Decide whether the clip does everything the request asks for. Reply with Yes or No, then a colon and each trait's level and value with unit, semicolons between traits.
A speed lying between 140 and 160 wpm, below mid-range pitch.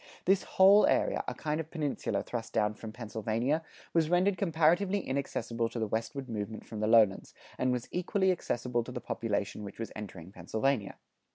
No: average, 175 wpm; low, 120 Hz